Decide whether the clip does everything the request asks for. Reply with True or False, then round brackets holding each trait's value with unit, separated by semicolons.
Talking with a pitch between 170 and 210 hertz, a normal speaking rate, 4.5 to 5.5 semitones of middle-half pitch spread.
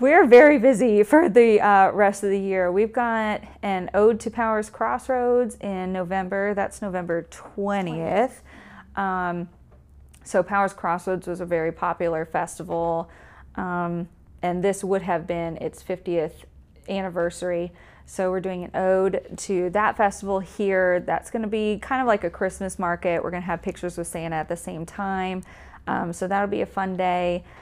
False (190 Hz; 165 wpm; 2.6 semitones)